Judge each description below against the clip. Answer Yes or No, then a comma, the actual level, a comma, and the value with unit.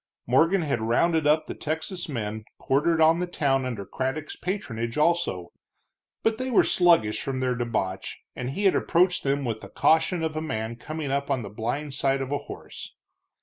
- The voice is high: No, medium, 140 Hz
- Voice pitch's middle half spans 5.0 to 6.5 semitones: Yes, average, 5.3 semitones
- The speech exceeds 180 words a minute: Yes, average, 190 wpm